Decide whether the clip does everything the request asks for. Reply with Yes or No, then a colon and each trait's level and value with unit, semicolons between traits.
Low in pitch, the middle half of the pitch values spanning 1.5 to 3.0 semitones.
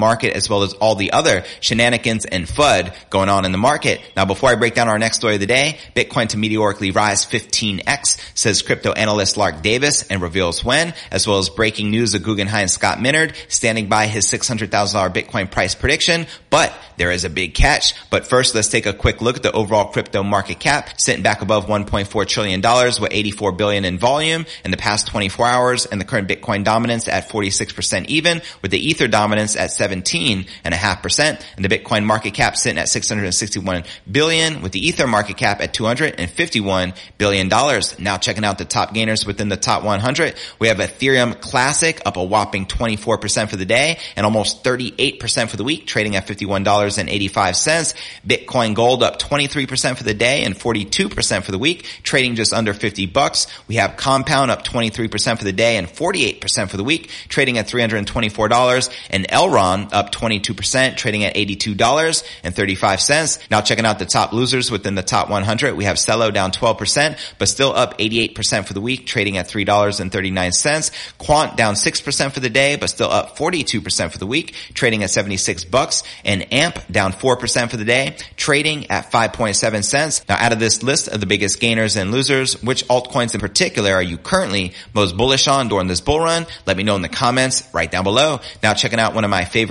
No: low, 110 Hz; average, 3.6 semitones